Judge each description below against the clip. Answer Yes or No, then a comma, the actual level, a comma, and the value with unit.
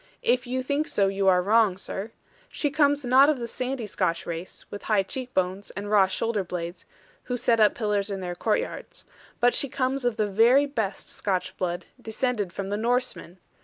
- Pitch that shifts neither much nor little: Yes, average, 4.6 semitones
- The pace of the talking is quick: No, average, 195 wpm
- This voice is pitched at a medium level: No, high, 215 Hz